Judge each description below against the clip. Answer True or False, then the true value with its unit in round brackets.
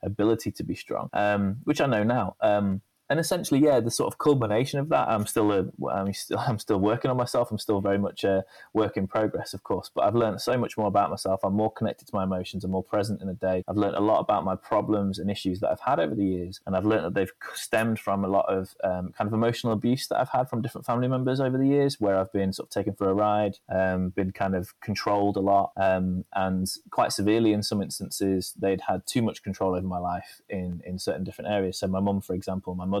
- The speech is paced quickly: True (260 wpm)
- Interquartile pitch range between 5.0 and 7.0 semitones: False (2.5 semitones)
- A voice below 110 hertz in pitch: True (100 Hz)